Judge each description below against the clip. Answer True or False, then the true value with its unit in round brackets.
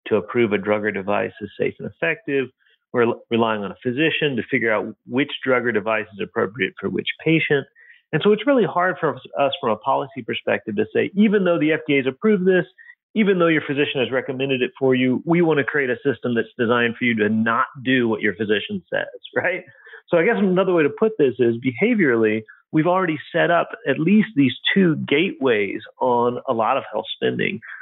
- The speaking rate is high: True (215 wpm)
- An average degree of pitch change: False (6.5 semitones)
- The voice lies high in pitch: False (140 Hz)